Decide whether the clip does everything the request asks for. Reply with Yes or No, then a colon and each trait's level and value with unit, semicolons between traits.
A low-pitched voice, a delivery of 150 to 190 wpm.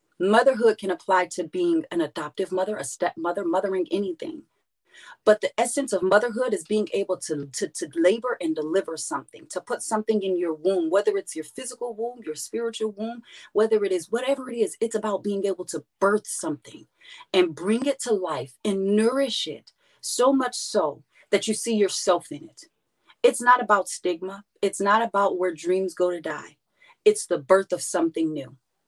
No: high, 205 Hz; average, 185 wpm